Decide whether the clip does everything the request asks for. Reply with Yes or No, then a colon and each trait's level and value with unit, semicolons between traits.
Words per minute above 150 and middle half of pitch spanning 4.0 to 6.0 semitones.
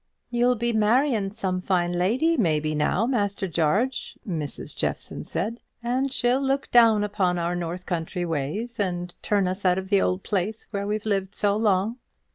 Yes: average, 170 wpm; average, 4.4 semitones